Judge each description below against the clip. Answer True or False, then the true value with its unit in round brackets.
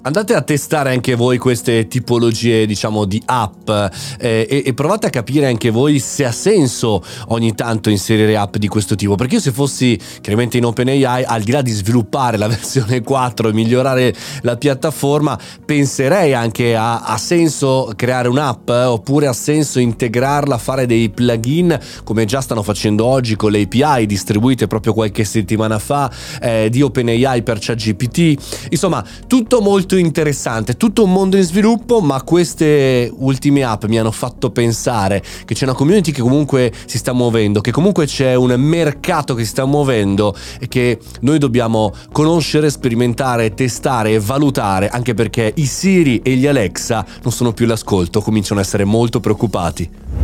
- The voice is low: True (125 Hz)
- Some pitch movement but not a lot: True (4.1 semitones)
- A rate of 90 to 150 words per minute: False (165 wpm)